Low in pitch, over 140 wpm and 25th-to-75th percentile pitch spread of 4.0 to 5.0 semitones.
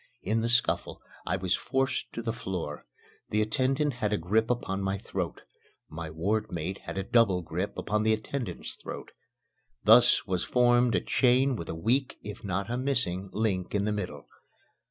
Yes: low, 105 Hz; average, 175 wpm; average, 4.7 semitones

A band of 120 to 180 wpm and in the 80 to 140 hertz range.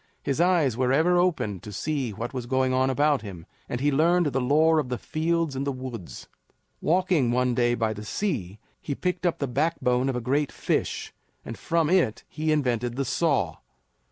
No: average, 195 wpm; low, 135 Hz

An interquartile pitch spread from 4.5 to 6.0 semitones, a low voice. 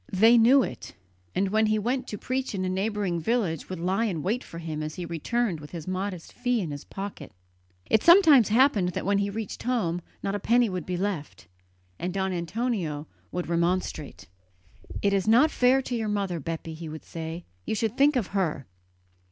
No: average, 5.1 semitones; high, 195 Hz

